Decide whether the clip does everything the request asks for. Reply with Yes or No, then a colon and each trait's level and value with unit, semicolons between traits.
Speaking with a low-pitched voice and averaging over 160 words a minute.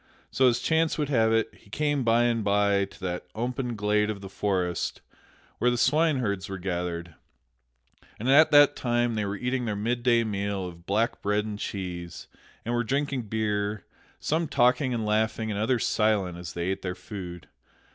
Yes: low, 110 Hz; average, 180 wpm